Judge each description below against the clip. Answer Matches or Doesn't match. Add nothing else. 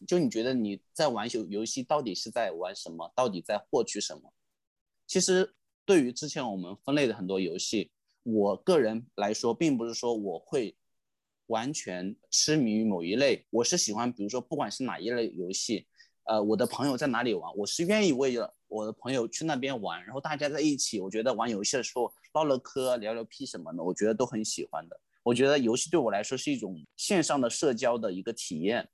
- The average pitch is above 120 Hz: Doesn't match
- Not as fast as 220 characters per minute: Doesn't match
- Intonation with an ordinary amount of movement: Matches